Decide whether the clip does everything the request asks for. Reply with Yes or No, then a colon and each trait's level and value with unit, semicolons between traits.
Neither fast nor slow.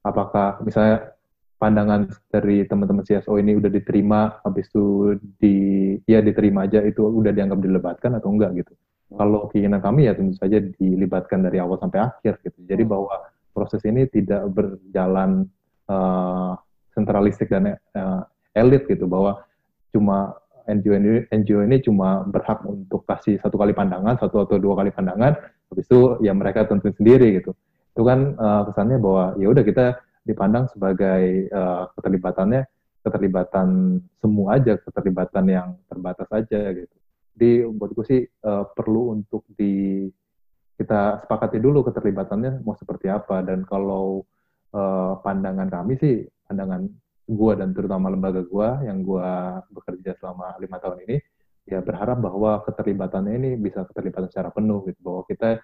No: fast, 145 wpm